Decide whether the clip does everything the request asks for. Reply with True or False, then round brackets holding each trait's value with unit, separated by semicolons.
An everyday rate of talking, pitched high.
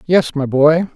False (190 wpm; 155 Hz)